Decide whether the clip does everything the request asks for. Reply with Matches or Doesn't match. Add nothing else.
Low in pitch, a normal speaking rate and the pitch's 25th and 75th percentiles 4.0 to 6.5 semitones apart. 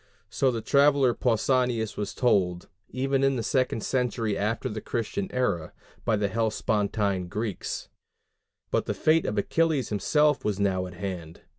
Matches